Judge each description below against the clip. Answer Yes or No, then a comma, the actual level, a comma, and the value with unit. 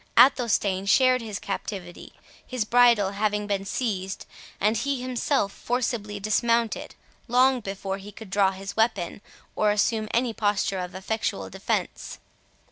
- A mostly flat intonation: No, average, 3.2 semitones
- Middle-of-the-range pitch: No, high, 210 Hz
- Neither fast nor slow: No, slow, 130 wpm